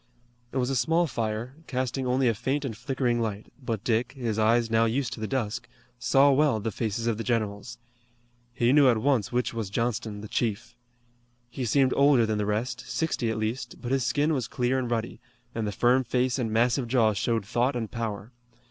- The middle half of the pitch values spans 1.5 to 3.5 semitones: Yes, average, 2.8 semitones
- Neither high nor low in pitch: No, low, 120 Hz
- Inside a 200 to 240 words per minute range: Yes, fast, 205 wpm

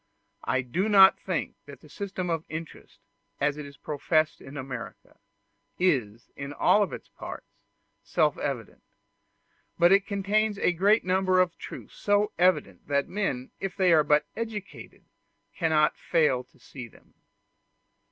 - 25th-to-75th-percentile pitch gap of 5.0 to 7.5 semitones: Yes, wide, 5.4 semitones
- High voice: No, medium, 165 Hz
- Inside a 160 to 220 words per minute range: No, average, 145 wpm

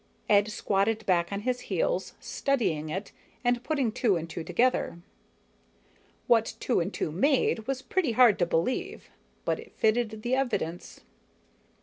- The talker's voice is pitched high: Yes, high, 220 Hz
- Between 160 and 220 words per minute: No, average, 145 wpm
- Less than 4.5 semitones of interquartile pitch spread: No, average, 5.3 semitones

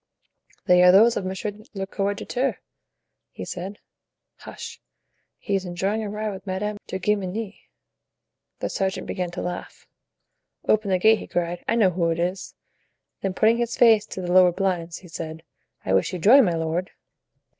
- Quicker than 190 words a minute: No, average, 170 wpm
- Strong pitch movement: No, average, 2.9 semitones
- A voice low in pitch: No, high, 190 Hz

